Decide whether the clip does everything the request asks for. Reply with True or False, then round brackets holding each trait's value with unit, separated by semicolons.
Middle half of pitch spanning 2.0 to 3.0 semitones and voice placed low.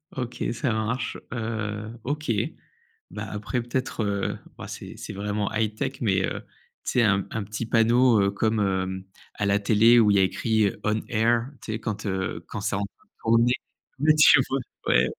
True (2.6 semitones; 110 Hz)